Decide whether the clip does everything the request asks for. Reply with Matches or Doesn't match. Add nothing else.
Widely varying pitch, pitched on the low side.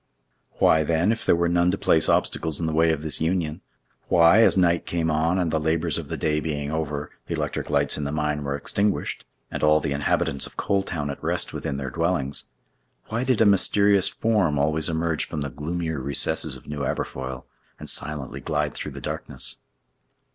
Doesn't match